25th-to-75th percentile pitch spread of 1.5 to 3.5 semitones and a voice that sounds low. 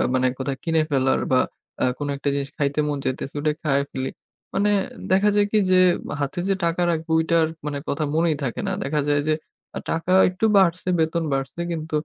No: average, 3.2 semitones; medium, 155 Hz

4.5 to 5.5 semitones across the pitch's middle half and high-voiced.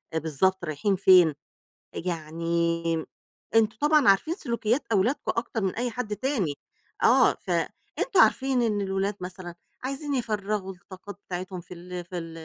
Yes: average, 4.8 semitones; high, 195 Hz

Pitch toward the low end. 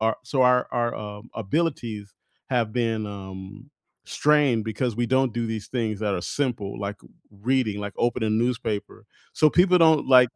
Yes: low, 115 Hz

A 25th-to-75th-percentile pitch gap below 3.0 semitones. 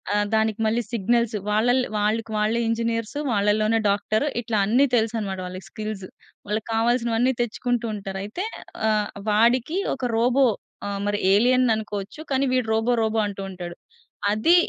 Yes: narrow, 2.5 semitones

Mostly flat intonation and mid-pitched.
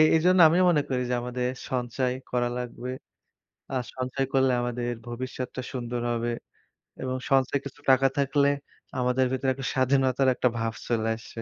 No: narrow, 1.7 semitones; low, 130 Hz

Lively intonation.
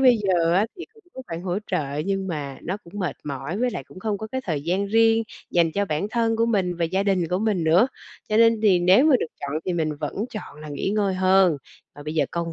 No: average, 4.5 semitones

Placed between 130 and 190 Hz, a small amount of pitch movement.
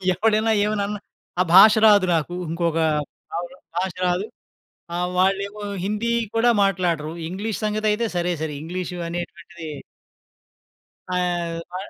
No: medium, 185 Hz; average, 3.2 semitones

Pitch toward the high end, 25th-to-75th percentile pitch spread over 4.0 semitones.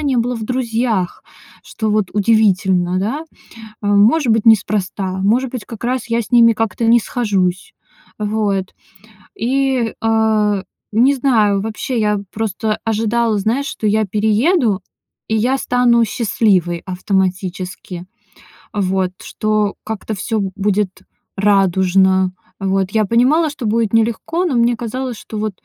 No: high, 215 Hz; average, 3.2 semitones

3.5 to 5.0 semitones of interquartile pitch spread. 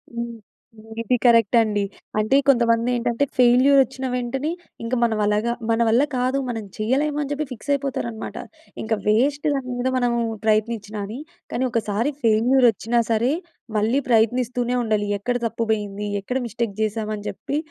No: average, 2.7 semitones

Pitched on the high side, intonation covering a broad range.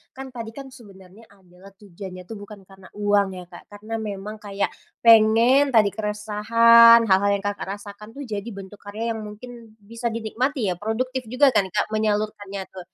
No: high, 210 Hz; narrow, 2.4 semitones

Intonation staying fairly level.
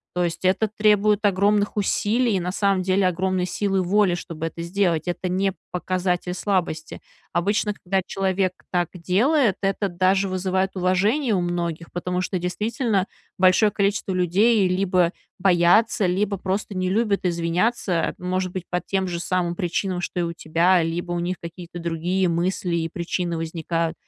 Yes: narrow, 2.1 semitones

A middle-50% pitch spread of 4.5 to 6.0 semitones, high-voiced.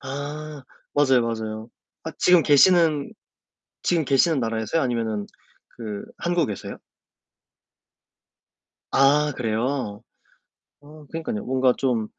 No: average, 5.1 semitones; low, 135 Hz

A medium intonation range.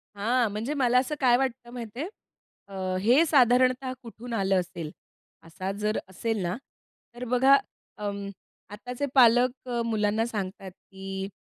Yes: average, 4.2 semitones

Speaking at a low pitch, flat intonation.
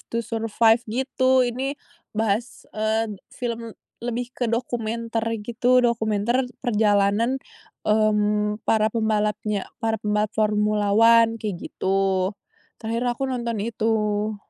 No: high, 220 Hz; narrow, 1.9 semitones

